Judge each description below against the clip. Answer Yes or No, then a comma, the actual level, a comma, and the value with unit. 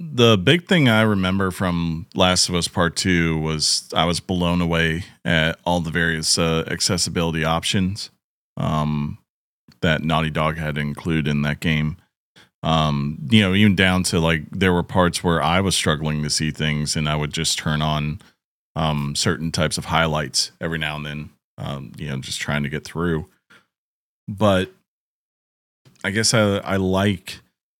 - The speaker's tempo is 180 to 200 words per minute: No, average, 170 wpm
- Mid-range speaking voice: No, very low, 80 Hz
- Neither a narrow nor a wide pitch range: Yes, average, 3.3 semitones